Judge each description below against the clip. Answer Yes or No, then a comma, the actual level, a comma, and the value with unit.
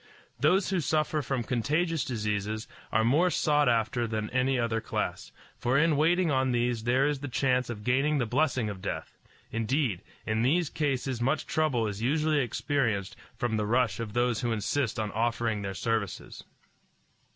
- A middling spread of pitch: Yes, average, 4.5 semitones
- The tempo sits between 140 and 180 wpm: Yes, average, 170 wpm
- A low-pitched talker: Yes, low, 125 Hz